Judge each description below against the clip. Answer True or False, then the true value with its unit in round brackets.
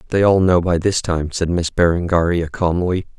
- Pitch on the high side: False (90 Hz)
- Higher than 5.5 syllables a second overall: False (4.9 syllables/s)